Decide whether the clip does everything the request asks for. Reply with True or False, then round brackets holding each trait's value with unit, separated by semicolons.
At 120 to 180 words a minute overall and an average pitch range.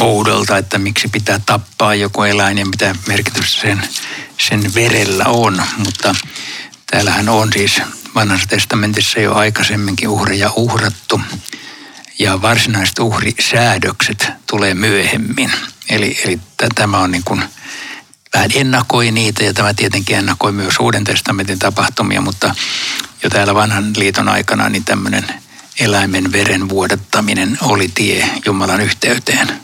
False (125 wpm; 1.9 semitones)